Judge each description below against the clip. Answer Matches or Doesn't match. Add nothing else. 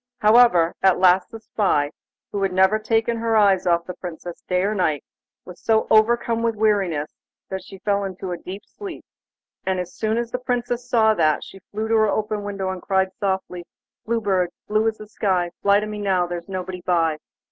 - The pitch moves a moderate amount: Matches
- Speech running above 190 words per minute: Matches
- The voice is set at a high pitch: Matches